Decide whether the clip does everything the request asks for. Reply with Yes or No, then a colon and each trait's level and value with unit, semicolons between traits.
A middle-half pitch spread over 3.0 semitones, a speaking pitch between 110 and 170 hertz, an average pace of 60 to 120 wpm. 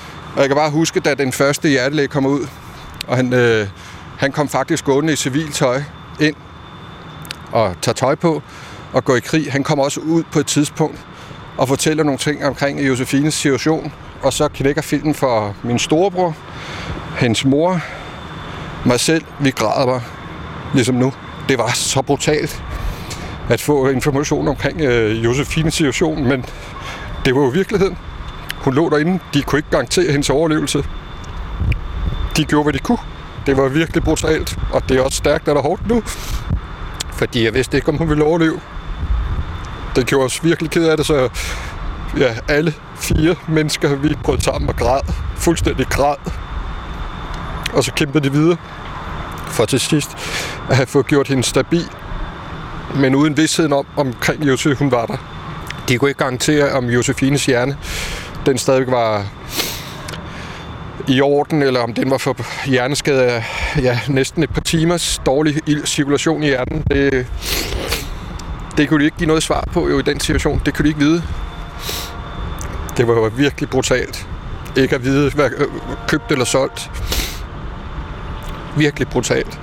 No: average, 3.8 semitones; medium, 140 Hz; average, 160 wpm